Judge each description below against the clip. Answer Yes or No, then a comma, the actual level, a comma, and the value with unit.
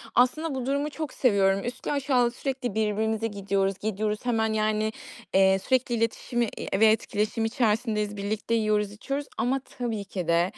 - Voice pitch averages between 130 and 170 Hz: No, high, 220 Hz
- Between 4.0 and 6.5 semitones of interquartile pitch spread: No, average, 3.0 semitones